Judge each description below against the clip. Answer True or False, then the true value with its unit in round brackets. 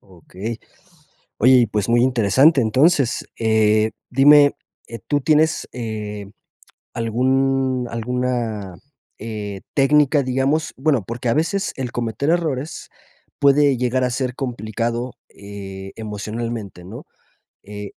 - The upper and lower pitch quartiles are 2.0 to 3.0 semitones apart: False (3.8 semitones)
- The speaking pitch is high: False (120 Hz)